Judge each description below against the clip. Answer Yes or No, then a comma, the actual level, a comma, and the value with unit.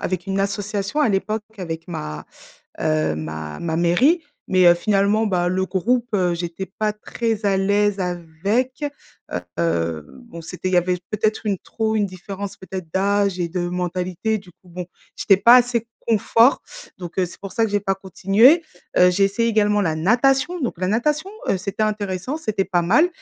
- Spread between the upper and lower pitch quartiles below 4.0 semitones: Yes, average, 3.5 semitones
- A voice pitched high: Yes, high, 195 Hz